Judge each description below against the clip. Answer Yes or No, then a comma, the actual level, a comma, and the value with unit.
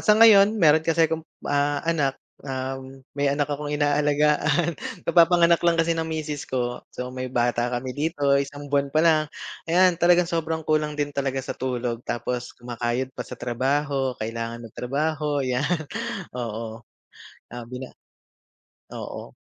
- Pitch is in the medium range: Yes, medium, 145 Hz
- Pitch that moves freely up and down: No, average, 4.2 semitones